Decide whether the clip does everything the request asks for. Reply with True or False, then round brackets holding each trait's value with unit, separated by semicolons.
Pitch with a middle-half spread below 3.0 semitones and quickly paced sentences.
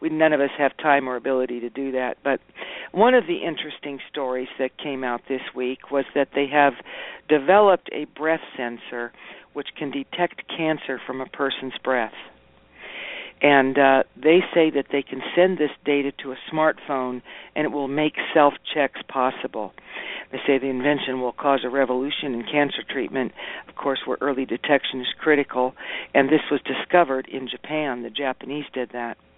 False (2.6 semitones; 175 wpm)